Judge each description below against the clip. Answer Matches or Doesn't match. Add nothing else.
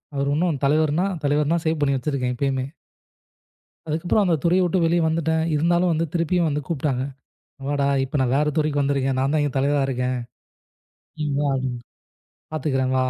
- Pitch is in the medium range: Matches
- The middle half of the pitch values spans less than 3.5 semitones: Matches